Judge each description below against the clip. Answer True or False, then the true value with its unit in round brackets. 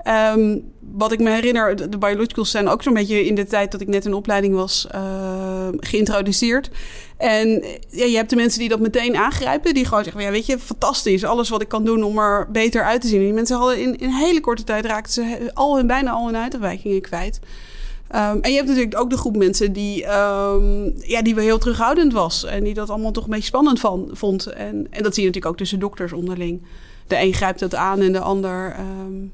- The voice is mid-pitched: False (210 Hz)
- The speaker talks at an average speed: False (235 wpm)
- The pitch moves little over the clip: False (3.1 semitones)